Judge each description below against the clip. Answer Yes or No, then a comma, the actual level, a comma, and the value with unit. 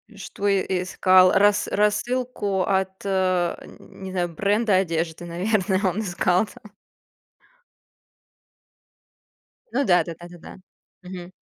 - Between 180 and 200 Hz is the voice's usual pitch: Yes, high, 190 Hz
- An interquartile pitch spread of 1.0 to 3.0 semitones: Yes, narrow, 2.4 semitones